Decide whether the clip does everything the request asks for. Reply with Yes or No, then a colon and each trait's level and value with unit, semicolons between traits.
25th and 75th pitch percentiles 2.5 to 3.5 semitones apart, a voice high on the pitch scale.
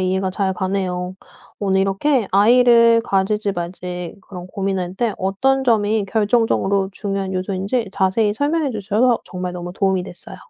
Yes: average, 2.9 semitones; high, 195 Hz